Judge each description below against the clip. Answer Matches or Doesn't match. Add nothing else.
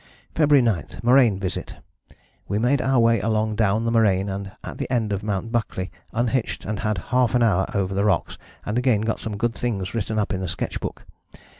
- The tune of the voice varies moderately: Matches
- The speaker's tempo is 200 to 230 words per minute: Matches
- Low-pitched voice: Matches